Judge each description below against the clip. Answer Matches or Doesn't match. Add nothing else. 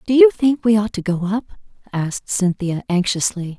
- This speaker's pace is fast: Doesn't match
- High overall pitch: Matches